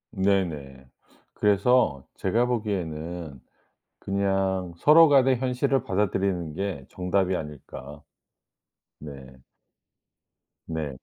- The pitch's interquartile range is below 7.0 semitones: Yes, average, 5.2 semitones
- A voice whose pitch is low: Yes, very low, 95 Hz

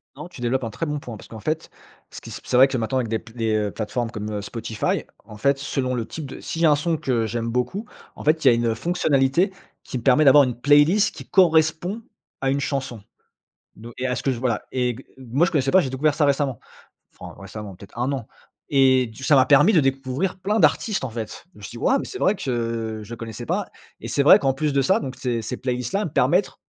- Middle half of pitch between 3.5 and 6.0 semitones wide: Yes, average, 4.1 semitones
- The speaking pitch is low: Yes, low, 130 Hz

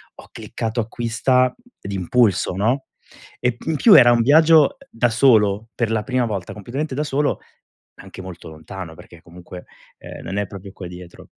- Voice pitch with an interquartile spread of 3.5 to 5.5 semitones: Yes, average, 4.9 semitones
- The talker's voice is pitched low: Yes, low, 115 Hz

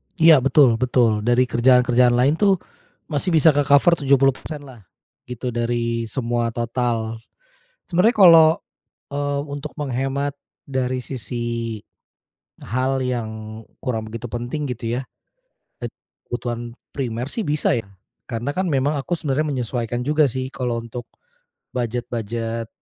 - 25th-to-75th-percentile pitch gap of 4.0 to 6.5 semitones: No, average, 3.2 semitones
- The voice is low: Yes, low, 125 Hz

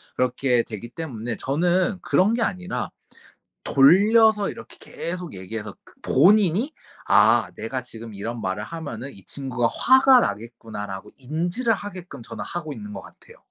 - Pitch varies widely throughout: Yes, wide, 8.4 semitones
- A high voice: No, medium, 140 Hz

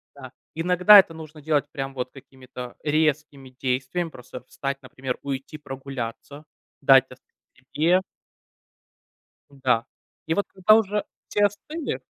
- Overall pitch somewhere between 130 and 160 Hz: Yes, medium, 140 Hz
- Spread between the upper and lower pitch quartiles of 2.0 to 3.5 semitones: No, average, 3.9 semitones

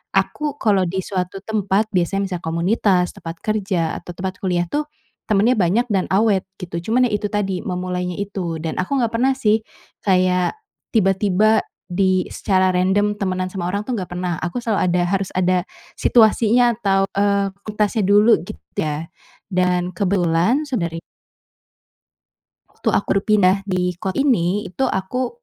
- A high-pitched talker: Yes, high, 195 Hz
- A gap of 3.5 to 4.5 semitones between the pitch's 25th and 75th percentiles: No, average, 2.9 semitones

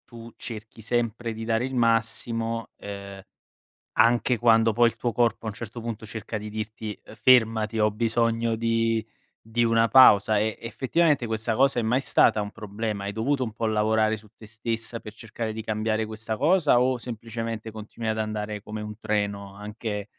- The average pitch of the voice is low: Yes, low, 110 Hz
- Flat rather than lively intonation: Yes, narrow, 1.4 semitones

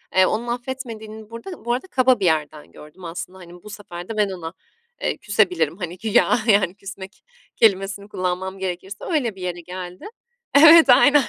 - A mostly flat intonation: No, average, 4.4 semitones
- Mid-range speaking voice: No, high, 195 Hz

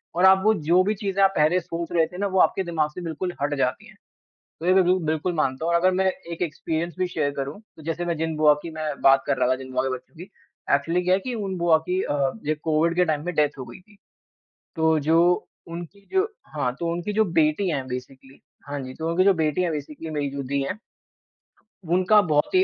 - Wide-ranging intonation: No, average, 3.7 semitones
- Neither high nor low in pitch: Yes, medium, 165 Hz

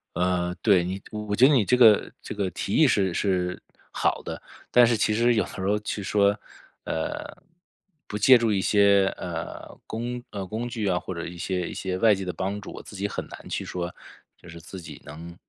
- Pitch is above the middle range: No, low, 100 Hz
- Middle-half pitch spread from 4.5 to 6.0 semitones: No, average, 3.1 semitones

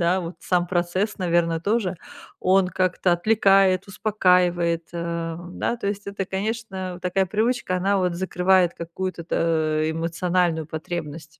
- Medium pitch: Yes, medium, 180 Hz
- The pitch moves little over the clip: Yes, narrow, 2.3 semitones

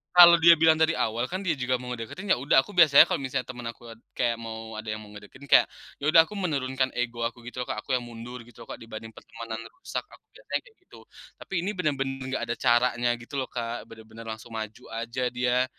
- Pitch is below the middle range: Yes, low, 125 Hz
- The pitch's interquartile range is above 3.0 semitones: Yes, average, 3.5 semitones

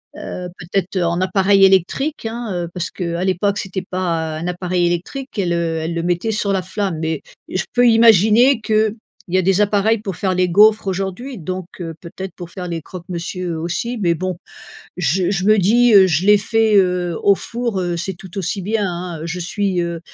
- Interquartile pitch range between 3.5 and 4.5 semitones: No, average, 3.1 semitones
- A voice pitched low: No, medium, 185 Hz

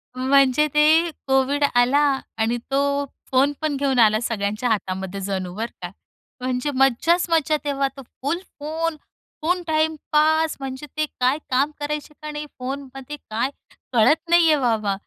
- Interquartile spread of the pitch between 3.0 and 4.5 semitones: Yes, average, 3.8 semitones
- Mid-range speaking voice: No, very high, 275 Hz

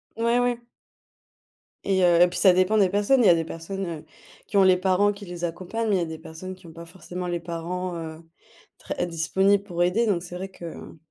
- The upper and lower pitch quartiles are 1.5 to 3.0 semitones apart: Yes, average, 2.7 semitones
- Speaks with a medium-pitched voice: Yes, medium, 180 Hz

